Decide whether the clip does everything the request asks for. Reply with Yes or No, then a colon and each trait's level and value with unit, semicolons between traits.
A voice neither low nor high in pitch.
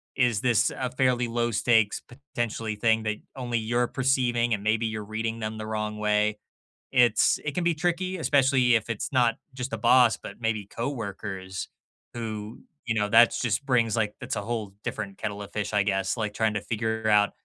No: low, 115 Hz